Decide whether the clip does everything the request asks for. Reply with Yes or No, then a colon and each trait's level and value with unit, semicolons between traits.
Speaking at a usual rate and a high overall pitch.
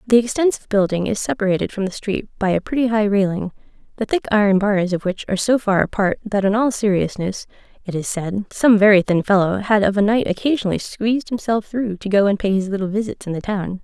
No: fast, 225 wpm; high, 205 Hz